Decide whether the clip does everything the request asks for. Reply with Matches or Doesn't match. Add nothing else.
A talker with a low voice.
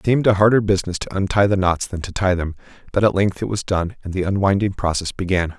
Matches